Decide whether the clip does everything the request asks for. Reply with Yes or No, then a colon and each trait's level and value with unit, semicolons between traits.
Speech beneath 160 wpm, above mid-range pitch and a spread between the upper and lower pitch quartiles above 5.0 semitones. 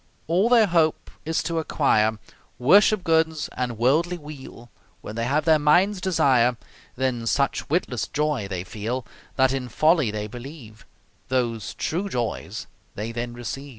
No: average, 150 wpm; low, 135 Hz; wide, 5.4 semitones